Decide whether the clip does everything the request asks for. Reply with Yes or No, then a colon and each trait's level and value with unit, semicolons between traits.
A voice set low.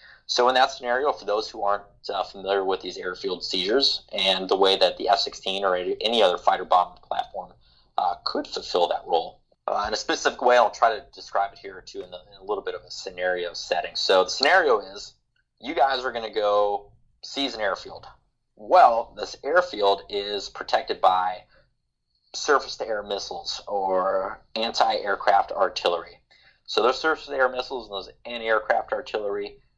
Yes: low, 110 Hz